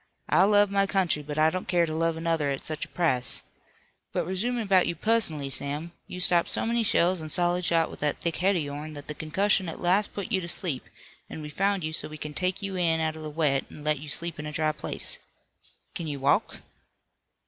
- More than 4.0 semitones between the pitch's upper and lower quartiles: No, average, 3.5 semitones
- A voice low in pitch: No, medium, 165 Hz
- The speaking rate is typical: No, fast, 235 wpm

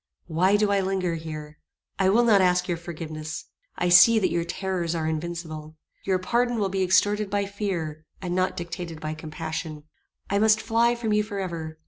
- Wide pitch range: No, average, 4.0 semitones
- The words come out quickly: No, average, 180 wpm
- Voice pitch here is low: No, medium, 180 Hz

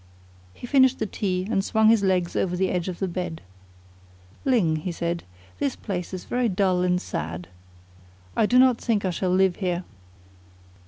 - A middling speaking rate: Yes, average, 175 wpm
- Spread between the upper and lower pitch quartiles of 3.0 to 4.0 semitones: Yes, average, 3.6 semitones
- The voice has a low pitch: No, medium, 185 Hz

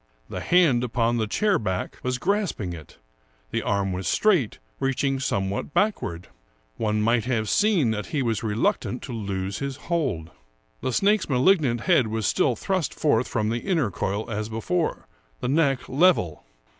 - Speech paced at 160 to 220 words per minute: Yes, average, 165 wpm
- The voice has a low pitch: Yes, low, 120 Hz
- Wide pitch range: Yes, wide, 6.7 semitones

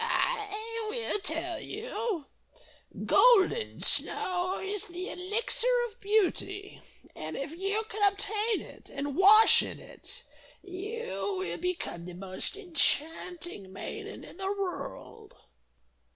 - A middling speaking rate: No, slow, 115 wpm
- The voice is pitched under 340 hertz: No, very high, 390 Hz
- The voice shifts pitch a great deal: No, average, 3.9 semitones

